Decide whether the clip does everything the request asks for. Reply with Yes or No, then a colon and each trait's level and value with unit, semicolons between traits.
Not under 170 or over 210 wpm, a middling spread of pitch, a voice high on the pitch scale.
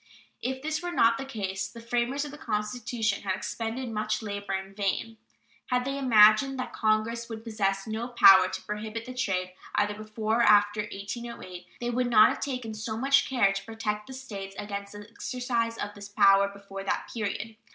Yes: average, 190 wpm; average, 3.0 semitones; high, 220 Hz